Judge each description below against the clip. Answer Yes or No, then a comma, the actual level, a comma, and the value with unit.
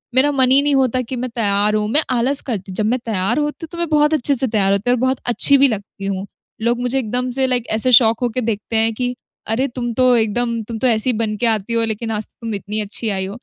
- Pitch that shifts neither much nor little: Yes, average, 3.2 semitones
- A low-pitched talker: No, high, 235 Hz